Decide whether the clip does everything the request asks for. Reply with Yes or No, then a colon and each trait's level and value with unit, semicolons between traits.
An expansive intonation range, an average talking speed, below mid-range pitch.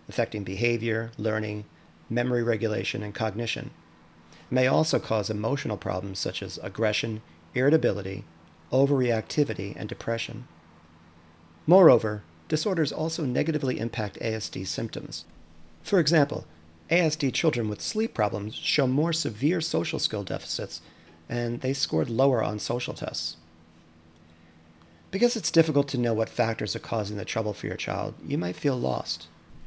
No: wide, 7.7 semitones; slow, 130 wpm; low, 110 Hz